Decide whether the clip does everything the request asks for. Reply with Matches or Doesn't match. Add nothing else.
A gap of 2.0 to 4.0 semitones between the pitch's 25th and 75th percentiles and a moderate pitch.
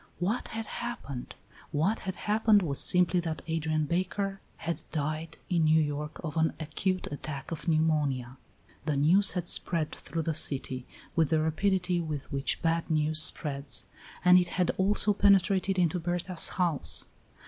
Matches